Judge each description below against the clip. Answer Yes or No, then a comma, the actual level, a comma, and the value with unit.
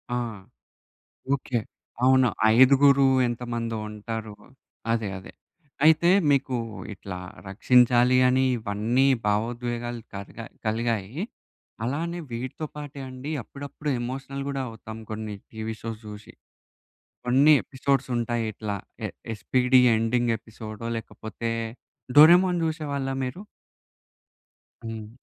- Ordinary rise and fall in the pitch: Yes, average, 3.5 semitones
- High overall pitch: No, low, 120 Hz